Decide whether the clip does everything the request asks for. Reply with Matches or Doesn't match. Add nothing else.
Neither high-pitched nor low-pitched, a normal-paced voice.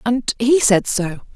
Doesn't match